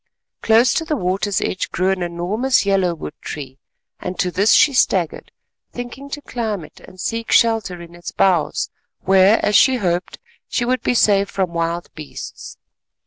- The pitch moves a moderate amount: Yes, average, 4.7 semitones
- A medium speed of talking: Yes, average, 165 wpm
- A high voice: Yes, high, 195 Hz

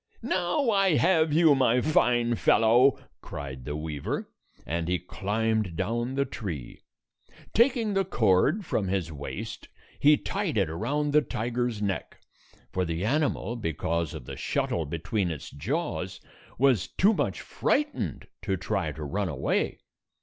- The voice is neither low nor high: No, low, 110 Hz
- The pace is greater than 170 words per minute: No, average, 140 wpm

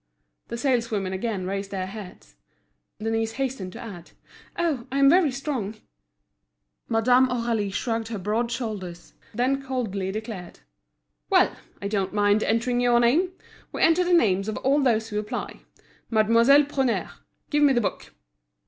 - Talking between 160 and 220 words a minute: No, average, 145 wpm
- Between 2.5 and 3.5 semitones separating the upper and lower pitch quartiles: No, average, 4.1 semitones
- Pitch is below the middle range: No, high, 230 Hz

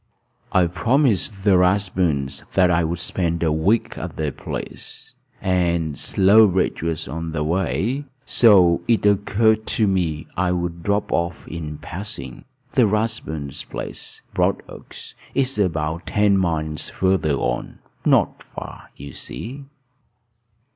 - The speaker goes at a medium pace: No, slow, 125 wpm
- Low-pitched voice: Yes, very low, 90 Hz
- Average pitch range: Yes, average, 4.2 semitones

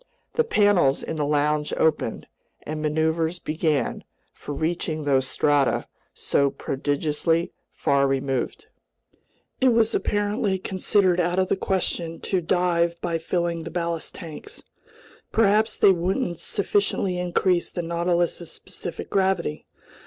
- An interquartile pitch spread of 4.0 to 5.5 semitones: No, average, 3.5 semitones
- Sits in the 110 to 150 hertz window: No, medium, 170 Hz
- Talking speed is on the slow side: Yes, slow, 125 wpm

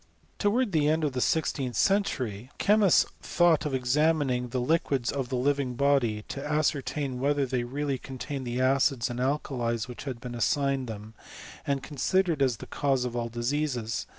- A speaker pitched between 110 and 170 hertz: Yes, low, 135 Hz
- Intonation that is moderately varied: Yes, average, 3.1 semitones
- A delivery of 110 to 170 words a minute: No, average, 180 wpm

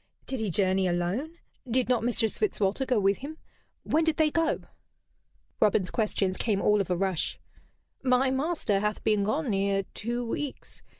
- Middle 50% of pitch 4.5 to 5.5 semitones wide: Yes, average, 5.2 semitones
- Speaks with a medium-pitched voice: No, high, 220 Hz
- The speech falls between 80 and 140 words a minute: No, average, 165 wpm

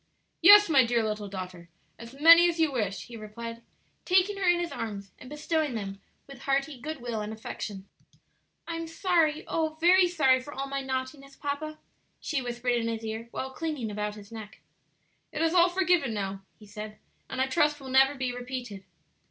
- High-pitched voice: Yes, very high, 260 Hz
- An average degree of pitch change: No, wide, 6.2 semitones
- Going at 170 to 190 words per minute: Yes, average, 185 wpm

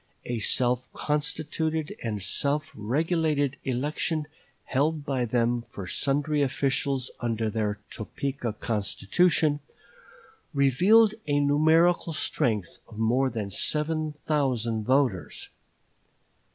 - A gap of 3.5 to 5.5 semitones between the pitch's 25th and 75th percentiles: Yes, average, 4.6 semitones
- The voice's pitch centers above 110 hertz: Yes, medium, 140 Hz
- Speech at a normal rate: No, slow, 100 wpm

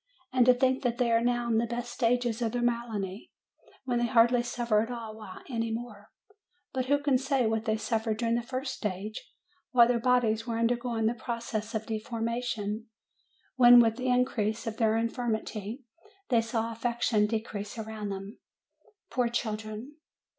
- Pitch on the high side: Yes, high, 230 Hz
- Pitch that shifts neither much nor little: No, narrow, 1.9 semitones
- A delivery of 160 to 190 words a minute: Yes, average, 170 wpm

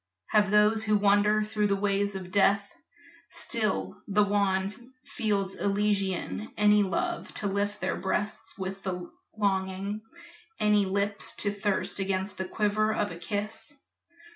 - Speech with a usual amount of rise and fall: No, narrow, 1.4 semitones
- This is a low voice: No, high, 205 Hz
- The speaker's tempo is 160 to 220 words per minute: No, slow, 135 wpm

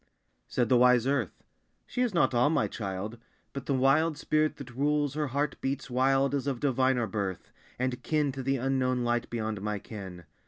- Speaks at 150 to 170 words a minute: No, average, 190 wpm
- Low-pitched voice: Yes, low, 130 Hz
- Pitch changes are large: No, average, 3.0 semitones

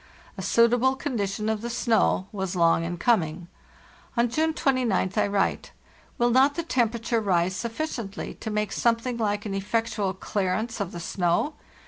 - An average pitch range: Yes, average, 3.8 semitones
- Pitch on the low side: No, high, 220 Hz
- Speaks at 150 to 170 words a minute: Yes, average, 155 wpm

